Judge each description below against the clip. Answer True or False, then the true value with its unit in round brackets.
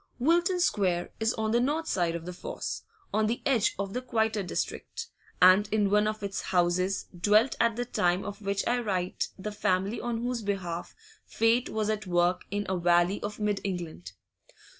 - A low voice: False (205 Hz)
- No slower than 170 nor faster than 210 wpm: True (185 wpm)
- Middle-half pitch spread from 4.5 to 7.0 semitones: False (3.7 semitones)